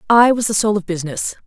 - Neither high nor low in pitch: No, high, 205 Hz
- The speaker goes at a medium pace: No, fast, 245 wpm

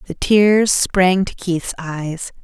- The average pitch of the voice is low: No, medium, 180 Hz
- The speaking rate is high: No, average, 150 wpm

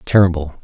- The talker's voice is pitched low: Yes, very low, 85 Hz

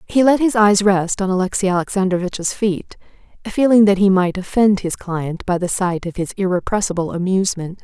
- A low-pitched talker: No, high, 190 Hz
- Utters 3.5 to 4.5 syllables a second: No, 5.5 syllables/s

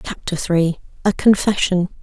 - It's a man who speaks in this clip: No, female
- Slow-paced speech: Yes, slow, 120 wpm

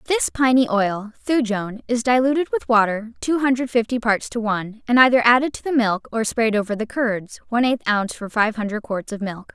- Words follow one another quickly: Yes, fast, 215 wpm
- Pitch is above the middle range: Yes, high, 230 Hz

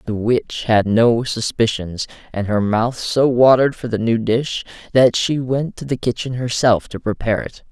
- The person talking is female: No, male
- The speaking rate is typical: Yes, average, 185 wpm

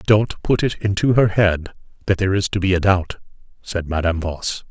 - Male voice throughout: Yes, male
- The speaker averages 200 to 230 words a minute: Yes, fast, 205 wpm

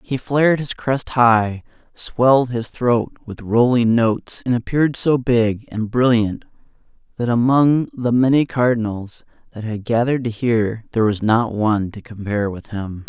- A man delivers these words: Yes, male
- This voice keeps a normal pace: Yes, average, 160 wpm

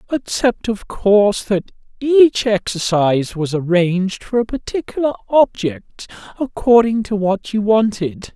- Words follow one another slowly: Yes, slow, 120 wpm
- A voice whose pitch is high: Yes, high, 210 Hz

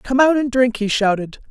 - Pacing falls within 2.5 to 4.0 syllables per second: No, 5.1 syllables/s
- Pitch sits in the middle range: No, high, 240 Hz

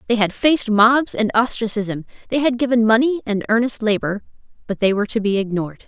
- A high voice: Yes, high, 220 Hz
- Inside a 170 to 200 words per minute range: Yes, average, 195 wpm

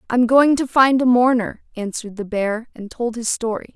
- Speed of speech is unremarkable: No, fast, 225 wpm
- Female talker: Yes, female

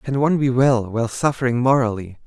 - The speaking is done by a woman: No, male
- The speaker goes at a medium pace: Yes, average, 185 wpm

